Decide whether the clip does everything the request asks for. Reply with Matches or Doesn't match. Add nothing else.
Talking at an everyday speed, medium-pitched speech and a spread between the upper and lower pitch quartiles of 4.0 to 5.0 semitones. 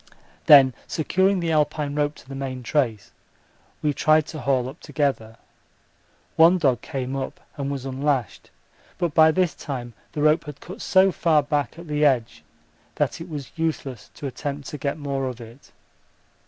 Doesn't match